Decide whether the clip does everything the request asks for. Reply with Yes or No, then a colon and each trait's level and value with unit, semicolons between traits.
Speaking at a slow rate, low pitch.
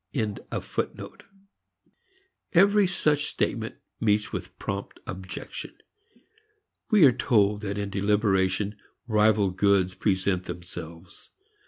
Yes: slow, 85 wpm; low, 100 Hz